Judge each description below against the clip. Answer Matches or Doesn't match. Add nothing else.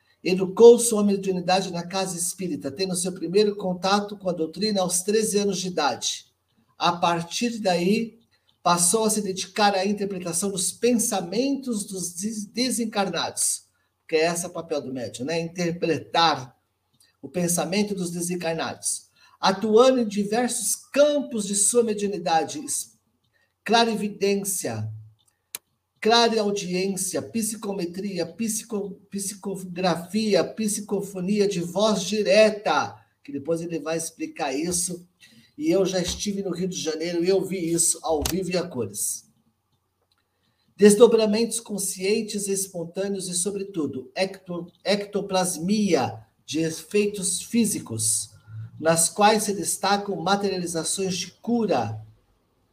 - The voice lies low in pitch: Doesn't match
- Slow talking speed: Matches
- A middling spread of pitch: Matches